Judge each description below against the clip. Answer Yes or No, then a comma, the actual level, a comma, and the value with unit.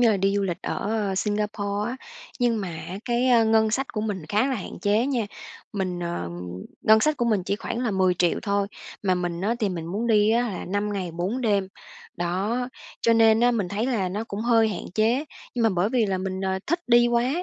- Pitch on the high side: Yes, high, 210 Hz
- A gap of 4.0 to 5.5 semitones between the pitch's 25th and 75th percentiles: No, average, 3.5 semitones